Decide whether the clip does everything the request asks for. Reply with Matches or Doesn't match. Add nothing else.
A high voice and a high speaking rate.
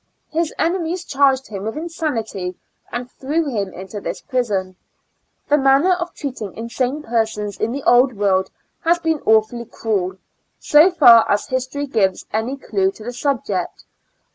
Doesn't match